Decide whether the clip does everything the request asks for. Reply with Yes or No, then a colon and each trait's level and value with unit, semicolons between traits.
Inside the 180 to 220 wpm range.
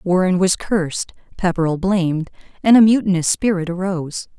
No: slow, 135 wpm